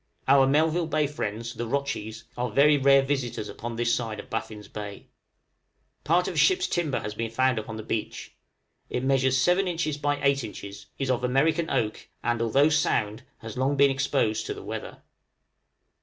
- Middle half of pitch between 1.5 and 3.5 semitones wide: No, average, 4.1 semitones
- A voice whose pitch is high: No, low, 130 Hz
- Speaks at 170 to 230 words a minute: Yes, average, 180 wpm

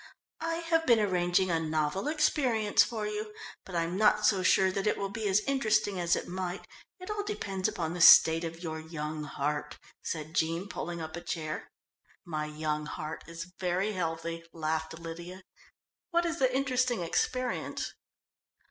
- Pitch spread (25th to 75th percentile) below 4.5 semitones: No, average, 4.8 semitones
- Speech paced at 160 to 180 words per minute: Yes, average, 165 wpm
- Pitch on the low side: No, medium, 180 Hz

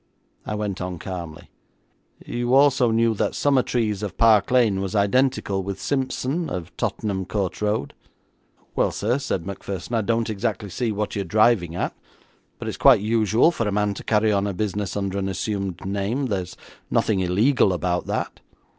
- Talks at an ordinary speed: Yes, average, 170 wpm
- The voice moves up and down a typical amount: Yes, average, 3.2 semitones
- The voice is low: Yes, low, 105 Hz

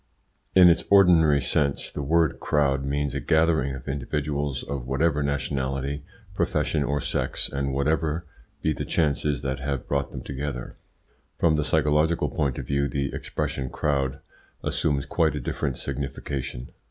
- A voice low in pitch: Yes, very low, 70 Hz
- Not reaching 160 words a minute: Yes, average, 150 wpm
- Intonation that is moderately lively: No, narrow, 2.0 semitones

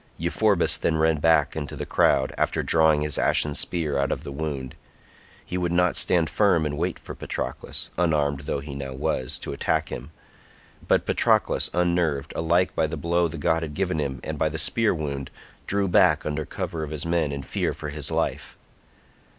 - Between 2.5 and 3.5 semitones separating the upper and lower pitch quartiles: Yes, average, 3.0 semitones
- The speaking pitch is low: Yes, very low, 80 Hz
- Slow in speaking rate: No, average, 190 wpm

